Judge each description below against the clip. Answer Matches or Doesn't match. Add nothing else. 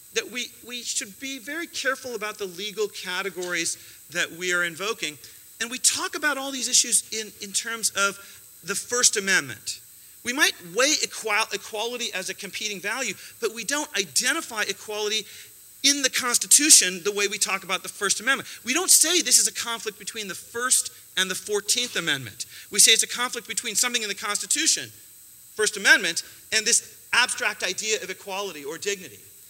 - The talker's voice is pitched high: Matches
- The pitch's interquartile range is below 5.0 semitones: Matches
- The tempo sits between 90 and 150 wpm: Doesn't match